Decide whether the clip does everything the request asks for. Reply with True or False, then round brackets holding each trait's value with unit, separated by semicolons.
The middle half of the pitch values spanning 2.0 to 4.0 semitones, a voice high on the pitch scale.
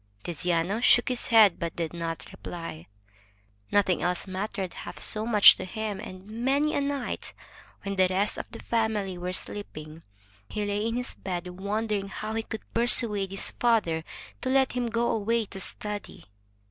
True (3.7 semitones; 205 Hz)